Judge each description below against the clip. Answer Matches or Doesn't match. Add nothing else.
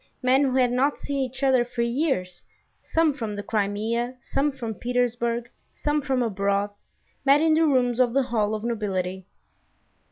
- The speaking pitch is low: Doesn't match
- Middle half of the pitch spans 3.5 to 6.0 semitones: Matches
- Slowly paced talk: Doesn't match